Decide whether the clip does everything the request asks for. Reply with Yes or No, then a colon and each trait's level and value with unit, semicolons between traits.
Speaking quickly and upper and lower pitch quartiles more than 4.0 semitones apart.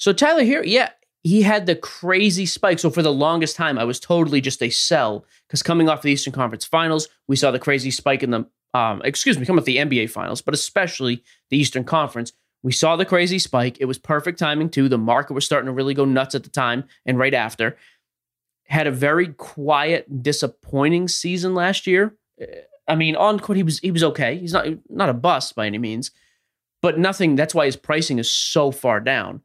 Yes: fast, 215 wpm; average, 4.7 semitones